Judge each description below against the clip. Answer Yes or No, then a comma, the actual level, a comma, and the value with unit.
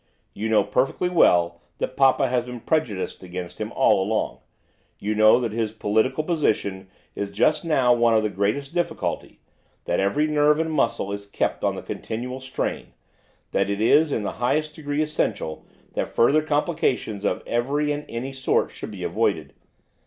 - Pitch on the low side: Yes, low, 125 Hz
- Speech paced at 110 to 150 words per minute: No, average, 170 wpm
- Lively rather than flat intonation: Yes, wide, 6.0 semitones